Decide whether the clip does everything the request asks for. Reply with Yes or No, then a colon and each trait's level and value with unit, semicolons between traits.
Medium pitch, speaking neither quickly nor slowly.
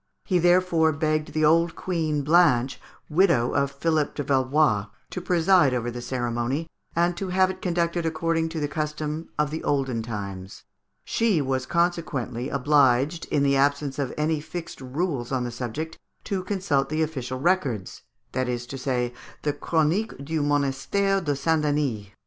Yes: medium, 150 Hz; average, 160 wpm